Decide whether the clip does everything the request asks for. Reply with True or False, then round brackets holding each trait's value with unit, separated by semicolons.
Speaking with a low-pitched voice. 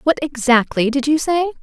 False (280 Hz)